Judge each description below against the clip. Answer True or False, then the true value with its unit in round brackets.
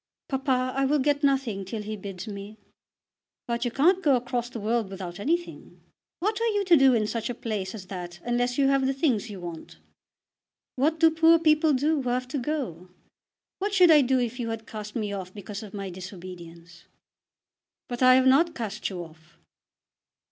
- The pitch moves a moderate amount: False (5.7 semitones)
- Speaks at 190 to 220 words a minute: True (195 wpm)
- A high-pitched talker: True (240 Hz)